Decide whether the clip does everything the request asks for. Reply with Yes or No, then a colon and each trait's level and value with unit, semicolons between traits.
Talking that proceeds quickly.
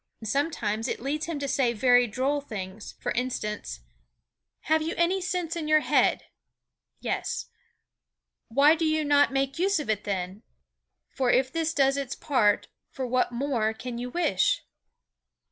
No: average, 155 wpm